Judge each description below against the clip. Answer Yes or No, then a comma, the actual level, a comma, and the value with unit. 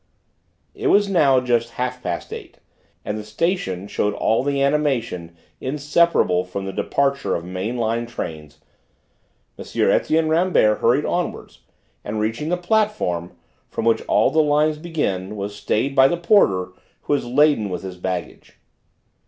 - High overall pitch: No, low, 125 Hz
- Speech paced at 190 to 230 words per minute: No, average, 150 wpm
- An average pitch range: No, wide, 7.4 semitones